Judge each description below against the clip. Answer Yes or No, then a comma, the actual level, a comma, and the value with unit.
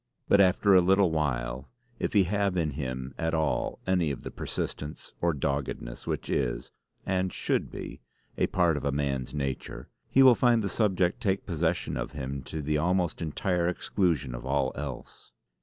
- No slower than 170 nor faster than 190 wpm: Yes, average, 175 wpm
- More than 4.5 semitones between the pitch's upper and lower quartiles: Yes, average, 5.2 semitones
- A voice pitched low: Yes, very low, 80 Hz